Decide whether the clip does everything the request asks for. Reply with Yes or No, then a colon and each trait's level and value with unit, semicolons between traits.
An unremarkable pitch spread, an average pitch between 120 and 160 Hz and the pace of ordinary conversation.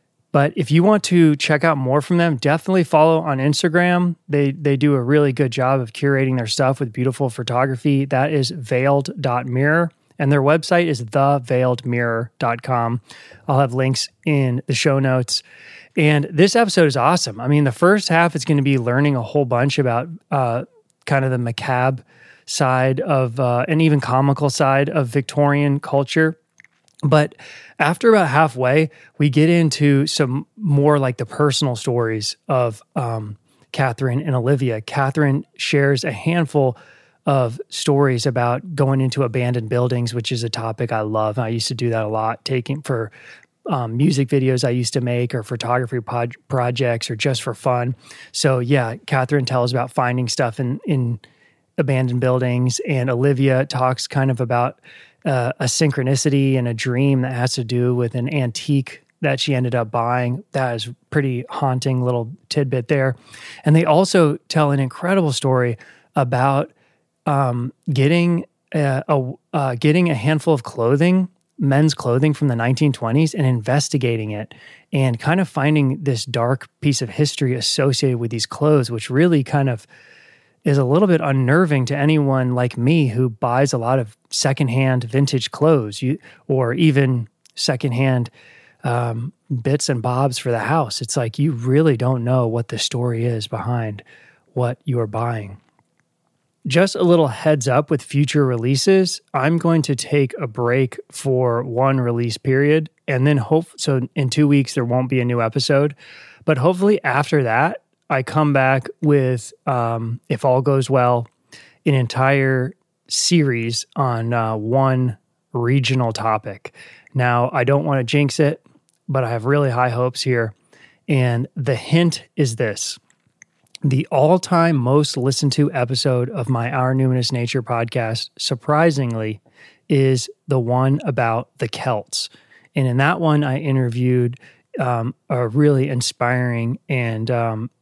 Yes: average, 3.2 semitones; low, 135 Hz; average, 160 wpm